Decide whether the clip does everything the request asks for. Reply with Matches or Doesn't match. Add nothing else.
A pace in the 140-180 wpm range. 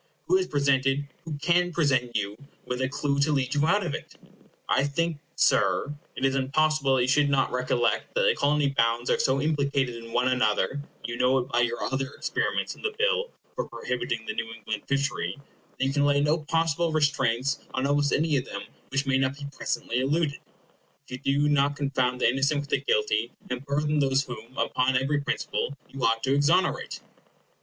Doesn't match